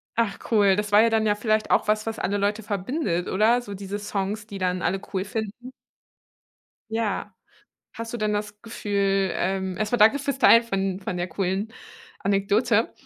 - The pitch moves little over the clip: Yes, narrow, 2.3 semitones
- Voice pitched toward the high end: Yes, high, 205 Hz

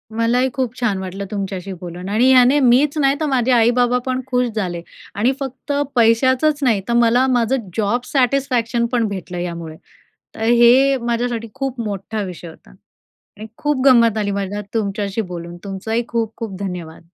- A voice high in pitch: Yes, high, 230 Hz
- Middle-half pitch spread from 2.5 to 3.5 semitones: No, average, 4.2 semitones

